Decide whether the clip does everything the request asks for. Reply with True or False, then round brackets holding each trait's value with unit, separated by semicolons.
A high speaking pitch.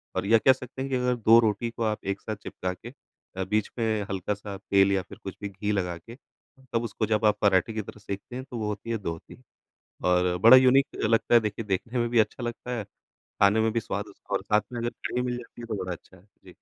False (105 Hz)